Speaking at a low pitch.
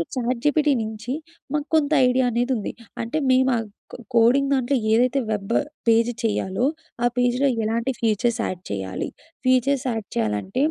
No: high, 240 Hz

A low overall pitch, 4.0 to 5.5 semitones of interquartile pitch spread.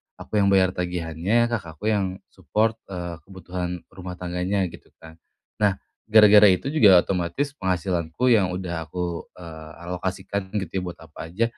No: very low, 90 Hz; average, 2.7 semitones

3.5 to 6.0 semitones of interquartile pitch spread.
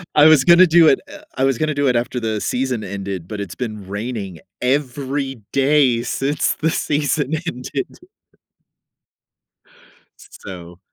Yes: average, 5.3 semitones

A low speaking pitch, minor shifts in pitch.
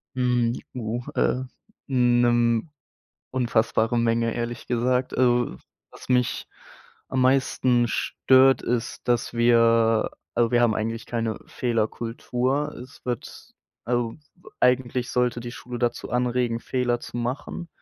Yes: low, 120 Hz; narrow, 1.3 semitones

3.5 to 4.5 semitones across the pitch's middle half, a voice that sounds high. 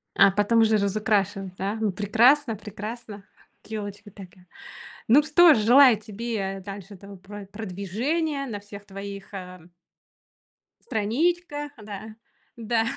No: average, 2.8 semitones; high, 210 Hz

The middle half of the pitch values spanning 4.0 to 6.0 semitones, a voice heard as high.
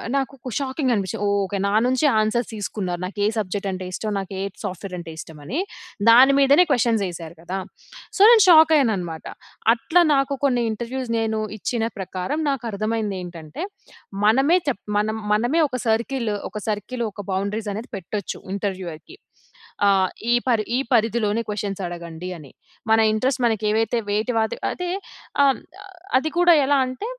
Yes: average, 4.8 semitones; high, 215 Hz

